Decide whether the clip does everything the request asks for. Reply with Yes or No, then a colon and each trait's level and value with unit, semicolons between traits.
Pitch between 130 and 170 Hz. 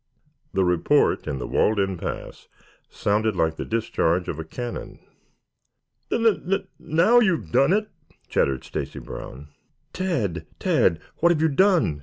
No: low, 110 Hz